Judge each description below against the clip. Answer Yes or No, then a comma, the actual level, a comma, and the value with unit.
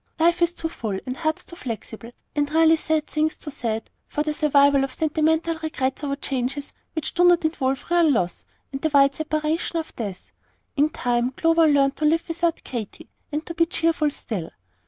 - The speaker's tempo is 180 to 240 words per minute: Yes, average, 190 wpm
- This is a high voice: Yes, very high, 305 Hz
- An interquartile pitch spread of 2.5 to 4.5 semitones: Yes, average, 3.3 semitones